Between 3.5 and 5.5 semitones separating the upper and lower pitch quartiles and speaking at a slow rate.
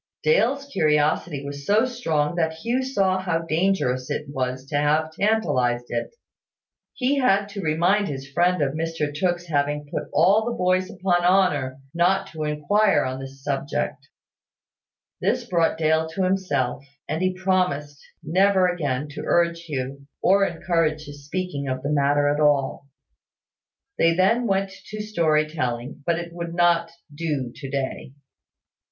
No: average, 4.5 semitones; average, 150 wpm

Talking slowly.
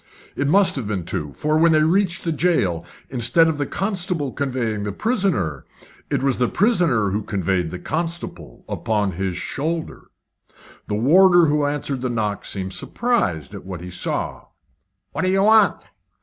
No: average, 165 wpm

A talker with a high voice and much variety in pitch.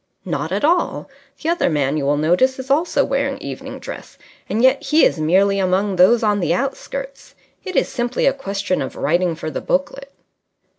Yes: high, 205 Hz; wide, 7.9 semitones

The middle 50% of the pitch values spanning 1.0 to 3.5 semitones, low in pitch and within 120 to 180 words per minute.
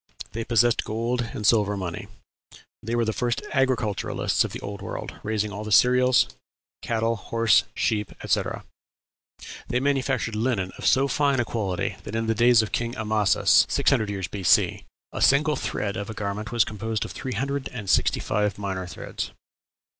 Yes: average, 2.9 semitones; low, 110 Hz; average, 170 wpm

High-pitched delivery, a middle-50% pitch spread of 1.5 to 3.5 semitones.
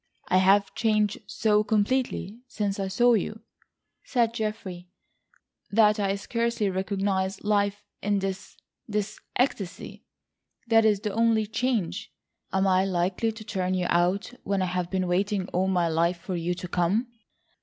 Yes: high, 200 Hz; narrow, 2.6 semitones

